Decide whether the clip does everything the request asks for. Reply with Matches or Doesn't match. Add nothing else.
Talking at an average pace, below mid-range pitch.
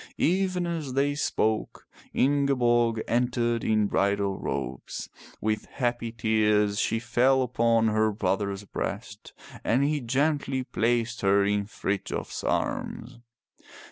Doesn't match